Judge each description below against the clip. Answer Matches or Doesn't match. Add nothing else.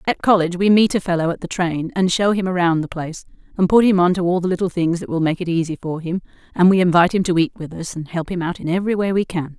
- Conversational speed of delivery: Doesn't match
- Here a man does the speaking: Doesn't match